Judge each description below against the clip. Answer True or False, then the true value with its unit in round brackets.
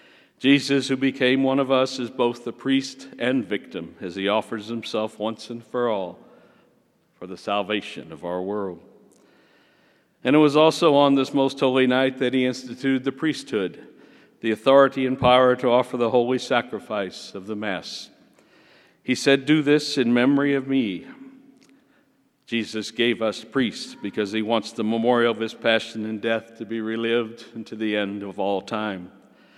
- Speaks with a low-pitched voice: True (120 Hz)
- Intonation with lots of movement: False (3.5 semitones)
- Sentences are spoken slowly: False (170 wpm)